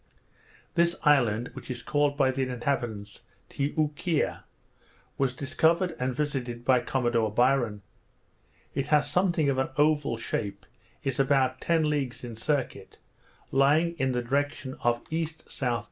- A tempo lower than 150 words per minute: Yes, average, 140 wpm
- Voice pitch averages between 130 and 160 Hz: Yes, low, 135 Hz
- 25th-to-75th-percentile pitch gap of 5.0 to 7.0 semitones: No, average, 3.5 semitones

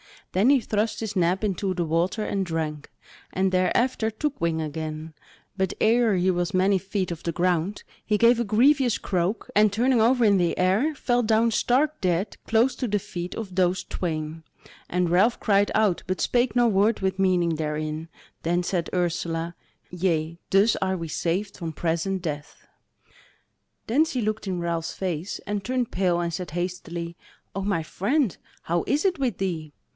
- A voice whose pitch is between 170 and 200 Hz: Yes, high, 190 Hz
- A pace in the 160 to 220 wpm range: Yes, average, 175 wpm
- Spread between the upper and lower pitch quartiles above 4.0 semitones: Yes, average, 4.4 semitones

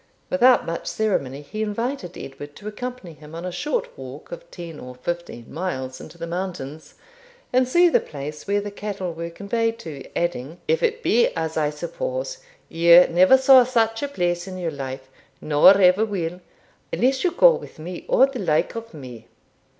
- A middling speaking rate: Yes, average, 180 wpm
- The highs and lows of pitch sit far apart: Yes, wide, 7.7 semitones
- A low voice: No, medium, 185 Hz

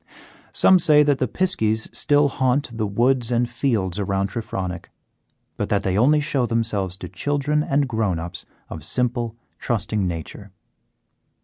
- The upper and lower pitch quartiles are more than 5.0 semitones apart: Yes, wide, 5.5 semitones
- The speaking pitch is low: Yes, low, 115 Hz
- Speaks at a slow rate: No, average, 145 wpm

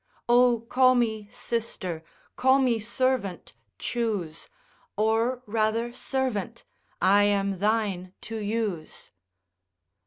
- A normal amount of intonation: Yes, average, 3.0 semitones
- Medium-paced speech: No, slow, 95 wpm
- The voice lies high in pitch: Yes, high, 225 Hz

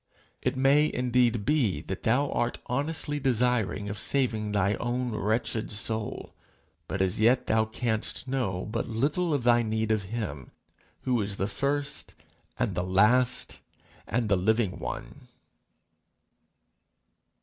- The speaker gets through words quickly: No, slow, 135 wpm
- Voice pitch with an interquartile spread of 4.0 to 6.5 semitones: No, average, 3.4 semitones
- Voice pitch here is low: Yes, low, 115 Hz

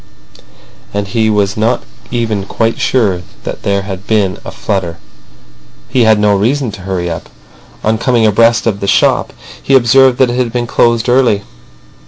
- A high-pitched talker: No, low, 110 Hz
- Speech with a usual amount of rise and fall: Yes, average, 3.2 semitones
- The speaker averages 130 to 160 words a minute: No, average, 170 wpm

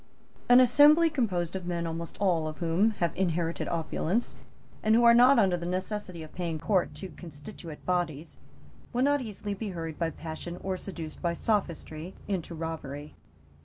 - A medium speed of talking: Yes, average, 165 wpm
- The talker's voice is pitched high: No, medium, 175 Hz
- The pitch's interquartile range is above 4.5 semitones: No, average, 4.2 semitones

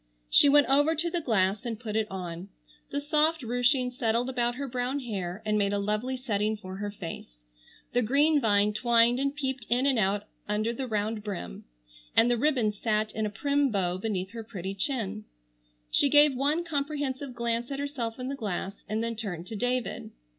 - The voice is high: Yes, high, 235 Hz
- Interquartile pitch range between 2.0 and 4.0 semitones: No, average, 4.6 semitones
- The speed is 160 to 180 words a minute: No, average, 195 wpm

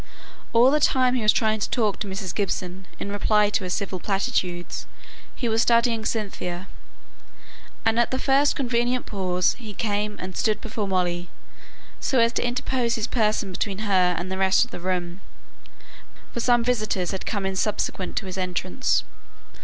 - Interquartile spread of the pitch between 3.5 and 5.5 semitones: Yes, average, 3.9 semitones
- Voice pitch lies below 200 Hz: No, high, 210 Hz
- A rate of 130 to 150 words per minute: No, average, 175 wpm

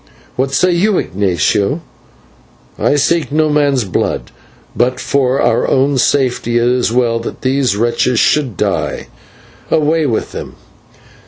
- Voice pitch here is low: Yes, low, 130 Hz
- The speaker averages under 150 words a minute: Yes, slow, 135 wpm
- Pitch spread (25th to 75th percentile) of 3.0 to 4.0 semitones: Yes, average, 3.7 semitones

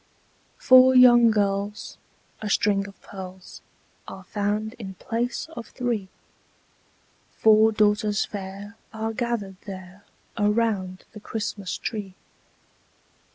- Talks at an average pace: No, slow, 105 wpm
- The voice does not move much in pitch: Yes, narrow, 2.3 semitones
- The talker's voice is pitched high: Yes, high, 210 Hz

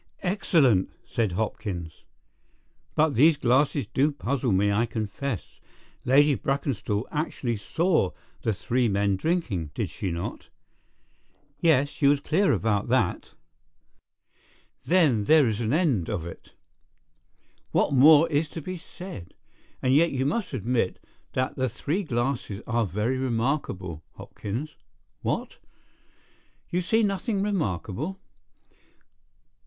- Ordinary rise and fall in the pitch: No, wide, 6.8 semitones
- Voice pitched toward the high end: No, low, 130 Hz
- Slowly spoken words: Yes, slow, 120 wpm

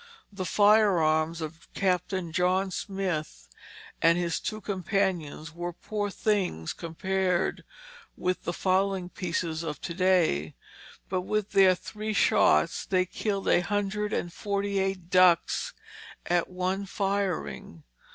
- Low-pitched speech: No, medium, 185 Hz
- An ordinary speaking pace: No, slow, 120 wpm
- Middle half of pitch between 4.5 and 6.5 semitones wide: No, average, 2.8 semitones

